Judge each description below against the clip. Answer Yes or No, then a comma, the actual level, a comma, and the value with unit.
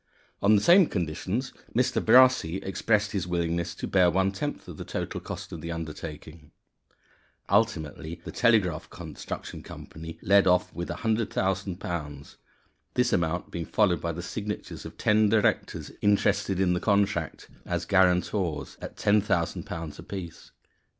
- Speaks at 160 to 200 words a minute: No, slow, 135 wpm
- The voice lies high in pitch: No, very low, 95 Hz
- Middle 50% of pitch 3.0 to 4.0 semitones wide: Yes, average, 3.6 semitones